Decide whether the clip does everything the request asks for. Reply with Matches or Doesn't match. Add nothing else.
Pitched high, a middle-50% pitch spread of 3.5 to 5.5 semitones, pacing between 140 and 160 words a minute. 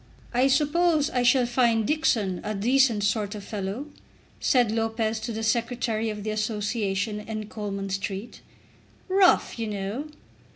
Doesn't match